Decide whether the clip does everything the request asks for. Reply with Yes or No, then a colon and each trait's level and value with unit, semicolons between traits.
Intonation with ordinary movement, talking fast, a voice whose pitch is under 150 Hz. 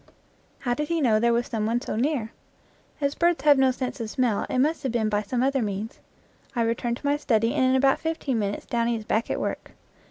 No: average, 3.3 semitones; fast, 235 wpm; high, 240 Hz